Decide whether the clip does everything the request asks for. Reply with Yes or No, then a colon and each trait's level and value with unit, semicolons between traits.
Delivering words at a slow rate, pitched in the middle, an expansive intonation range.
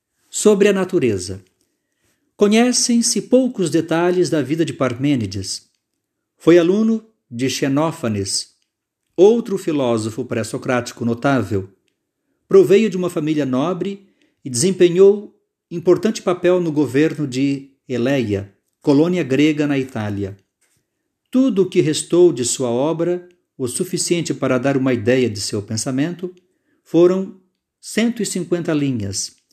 Yes: slow, 110 wpm; medium, 155 Hz; wide, 6.5 semitones